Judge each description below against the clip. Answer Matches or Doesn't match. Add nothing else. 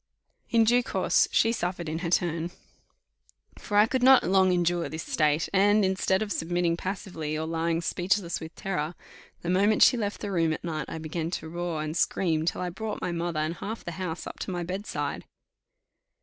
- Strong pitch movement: Doesn't match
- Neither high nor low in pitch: Matches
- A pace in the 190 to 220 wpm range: Matches